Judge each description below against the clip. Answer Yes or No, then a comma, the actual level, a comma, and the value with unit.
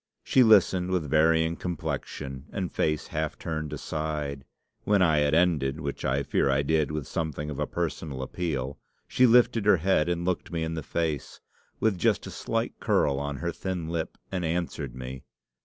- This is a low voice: Yes, very low, 80 Hz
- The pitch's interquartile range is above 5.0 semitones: No, average, 3.4 semitones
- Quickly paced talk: No, average, 180 wpm